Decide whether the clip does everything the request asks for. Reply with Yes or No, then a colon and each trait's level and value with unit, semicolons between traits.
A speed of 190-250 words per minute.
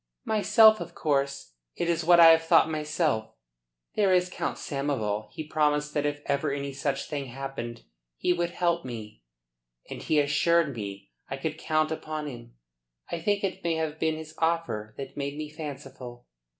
No: average, 175 wpm